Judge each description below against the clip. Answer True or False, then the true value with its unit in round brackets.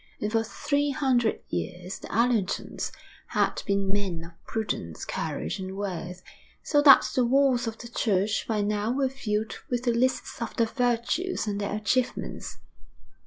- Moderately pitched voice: False (225 Hz)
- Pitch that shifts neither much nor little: True (3.8 semitones)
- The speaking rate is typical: True (160 wpm)